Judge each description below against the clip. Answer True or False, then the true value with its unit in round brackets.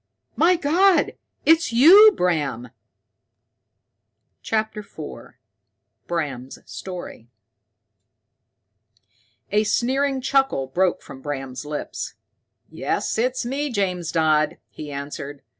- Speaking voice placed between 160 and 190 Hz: True (185 Hz)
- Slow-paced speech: True (90 wpm)